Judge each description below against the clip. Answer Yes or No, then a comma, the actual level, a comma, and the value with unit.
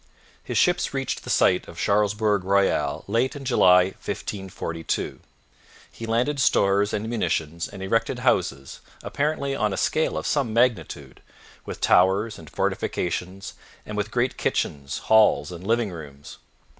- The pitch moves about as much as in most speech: Yes, average, 4.2 semitones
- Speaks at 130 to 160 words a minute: Yes, average, 140 wpm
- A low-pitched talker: Yes, low, 100 Hz